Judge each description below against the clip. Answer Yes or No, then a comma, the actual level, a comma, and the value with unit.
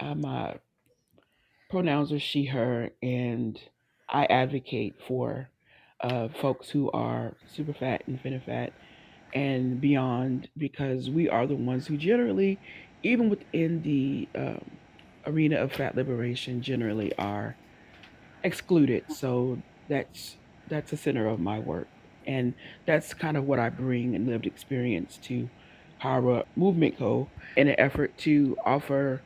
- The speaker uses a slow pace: Yes, slow, 130 wpm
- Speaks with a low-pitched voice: Yes, low, 130 Hz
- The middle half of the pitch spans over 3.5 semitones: No, average, 3.2 semitones